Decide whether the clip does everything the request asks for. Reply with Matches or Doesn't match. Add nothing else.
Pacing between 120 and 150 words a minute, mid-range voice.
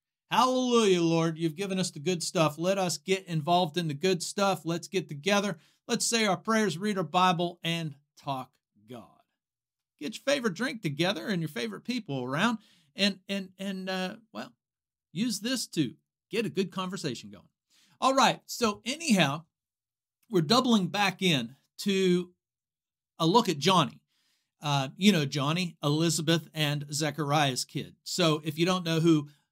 Doesn't match